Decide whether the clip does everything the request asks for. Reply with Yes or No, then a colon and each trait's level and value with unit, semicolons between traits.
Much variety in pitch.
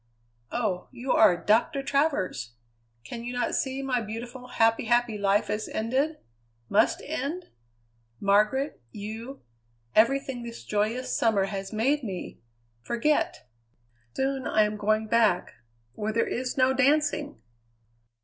No: average, 4.0 semitones